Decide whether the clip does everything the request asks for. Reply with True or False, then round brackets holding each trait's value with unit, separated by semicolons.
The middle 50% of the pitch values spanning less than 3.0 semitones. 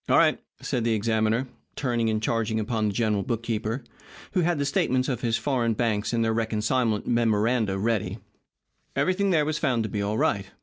True (2.6 semitones)